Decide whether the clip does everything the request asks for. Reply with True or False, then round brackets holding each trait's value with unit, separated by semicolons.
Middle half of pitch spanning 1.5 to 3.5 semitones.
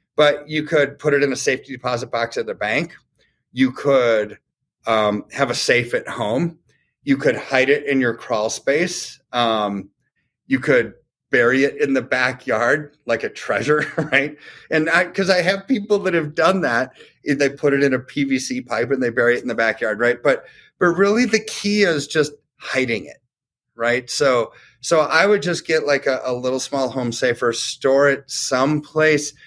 False (4.0 semitones)